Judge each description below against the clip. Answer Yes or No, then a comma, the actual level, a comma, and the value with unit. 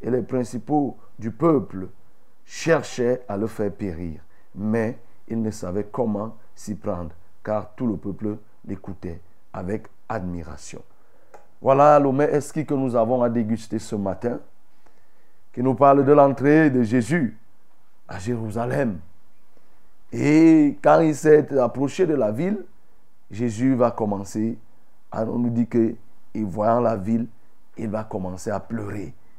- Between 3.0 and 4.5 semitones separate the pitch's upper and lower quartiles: Yes, average, 4.1 semitones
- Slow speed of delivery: Yes, slow, 135 wpm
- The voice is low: Yes, low, 115 Hz